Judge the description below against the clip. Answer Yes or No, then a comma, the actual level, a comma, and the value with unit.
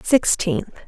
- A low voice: No, high, 220 Hz